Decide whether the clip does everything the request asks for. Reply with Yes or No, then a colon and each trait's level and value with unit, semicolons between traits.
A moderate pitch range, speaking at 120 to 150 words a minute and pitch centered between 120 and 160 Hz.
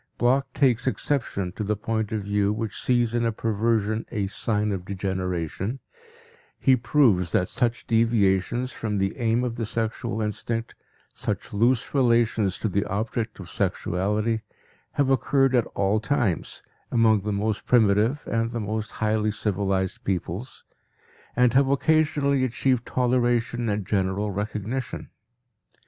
No: average, 3.1 semitones; average, 140 wpm; low, 110 Hz